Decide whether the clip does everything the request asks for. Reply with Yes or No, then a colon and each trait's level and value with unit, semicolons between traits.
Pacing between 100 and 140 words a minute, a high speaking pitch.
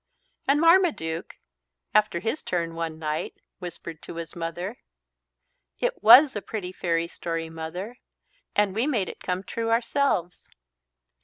No: slow, 135 wpm; medium, 180 Hz